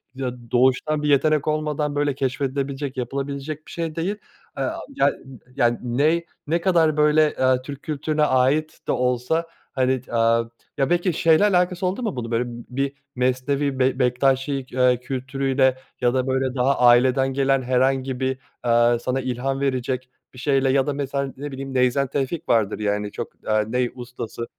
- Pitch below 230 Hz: Yes, low, 135 Hz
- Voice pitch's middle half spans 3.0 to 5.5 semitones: No, narrow, 2.5 semitones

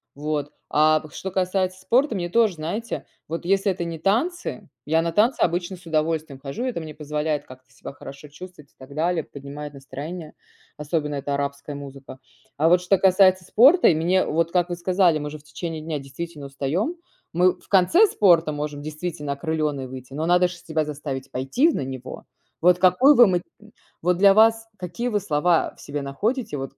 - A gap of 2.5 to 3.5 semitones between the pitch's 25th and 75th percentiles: No, average, 4.0 semitones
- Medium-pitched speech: Yes, medium, 165 Hz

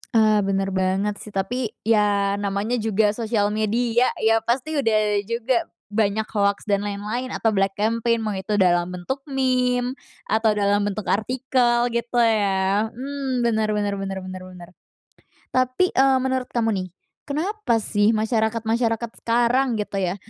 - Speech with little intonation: No, average, 3.3 semitones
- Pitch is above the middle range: Yes, high, 225 Hz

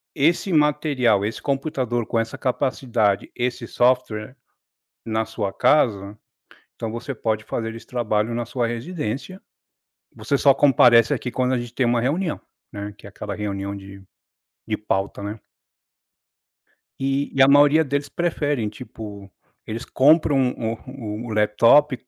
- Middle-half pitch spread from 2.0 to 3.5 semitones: No, average, 4.2 semitones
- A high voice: No, low, 120 Hz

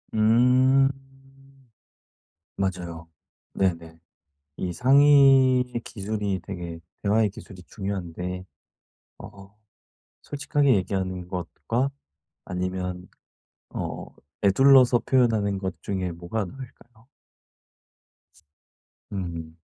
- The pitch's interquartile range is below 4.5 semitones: No, wide, 5.4 semitones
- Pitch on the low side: Yes, low, 100 Hz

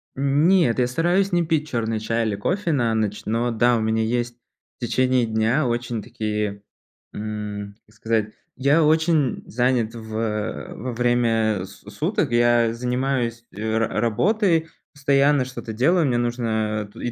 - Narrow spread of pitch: No, average, 3.7 semitones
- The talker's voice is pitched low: Yes, low, 120 Hz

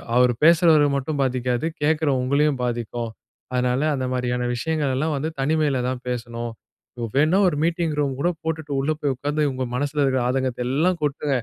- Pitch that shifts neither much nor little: Yes, average, 3.4 semitones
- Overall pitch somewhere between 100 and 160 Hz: Yes, medium, 140 Hz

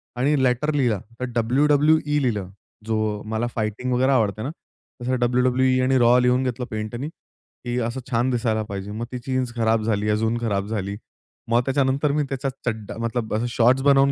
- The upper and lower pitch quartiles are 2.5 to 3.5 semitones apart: Yes, average, 2.9 semitones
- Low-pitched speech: Yes, low, 125 Hz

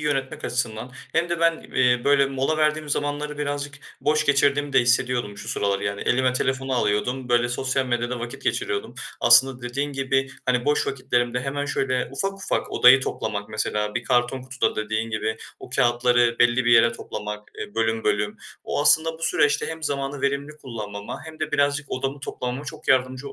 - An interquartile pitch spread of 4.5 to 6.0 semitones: No, average, 3.0 semitones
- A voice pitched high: No, low, 130 Hz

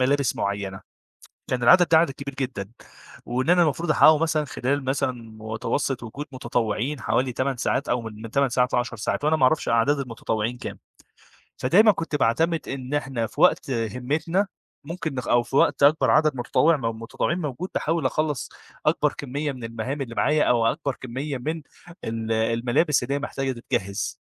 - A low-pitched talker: Yes, low, 130 Hz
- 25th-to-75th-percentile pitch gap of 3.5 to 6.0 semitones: Yes, average, 4.2 semitones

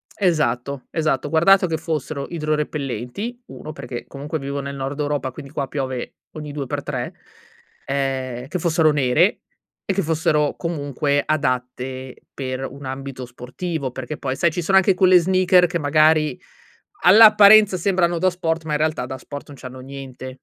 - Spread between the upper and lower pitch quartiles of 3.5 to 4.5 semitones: Yes, average, 4.1 semitones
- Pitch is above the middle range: No, medium, 150 Hz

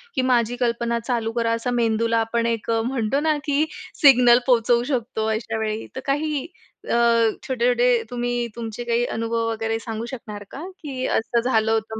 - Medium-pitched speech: No, high, 235 Hz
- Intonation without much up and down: Yes, narrow, 1.7 semitones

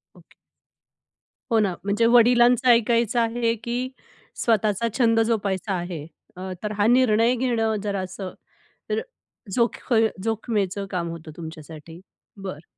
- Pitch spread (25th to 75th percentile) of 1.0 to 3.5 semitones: No, average, 3.9 semitones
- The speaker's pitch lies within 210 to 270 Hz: Yes, high, 215 Hz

